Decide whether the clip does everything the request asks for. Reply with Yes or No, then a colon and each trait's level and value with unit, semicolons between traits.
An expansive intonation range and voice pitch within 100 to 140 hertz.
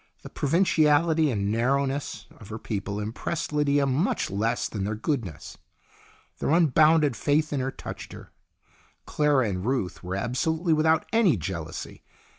Yes: wide, 6.6 semitones; low, 135 Hz